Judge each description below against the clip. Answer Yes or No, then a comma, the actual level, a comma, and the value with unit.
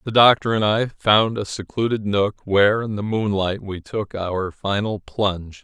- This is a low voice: Yes, low, 105 Hz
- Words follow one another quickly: No, average, 180 wpm